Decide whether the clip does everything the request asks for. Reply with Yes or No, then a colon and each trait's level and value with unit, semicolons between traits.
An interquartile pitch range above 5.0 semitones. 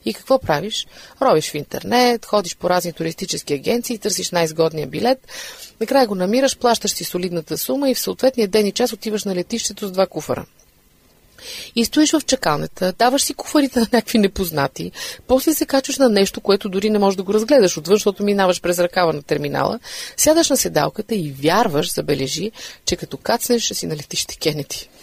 Yes: wide, 5.6 semitones